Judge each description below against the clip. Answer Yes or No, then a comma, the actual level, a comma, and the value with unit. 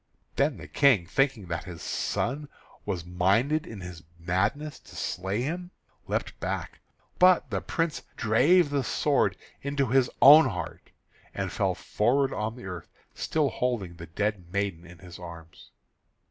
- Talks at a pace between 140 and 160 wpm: Yes, average, 150 wpm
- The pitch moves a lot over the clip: Yes, wide, 7.7 semitones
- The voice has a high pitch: No, low, 110 Hz